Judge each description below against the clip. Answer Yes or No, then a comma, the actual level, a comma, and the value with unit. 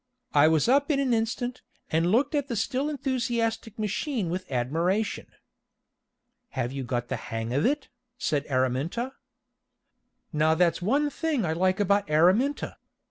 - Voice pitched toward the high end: Yes, high, 200 Hz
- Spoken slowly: No, average, 145 wpm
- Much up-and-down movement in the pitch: Yes, wide, 8.6 semitones